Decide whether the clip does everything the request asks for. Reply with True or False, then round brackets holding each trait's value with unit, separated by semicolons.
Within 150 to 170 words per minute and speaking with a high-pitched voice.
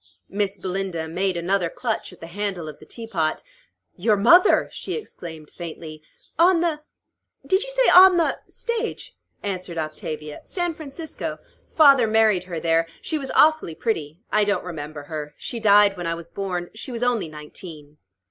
True (165 wpm; 195 Hz)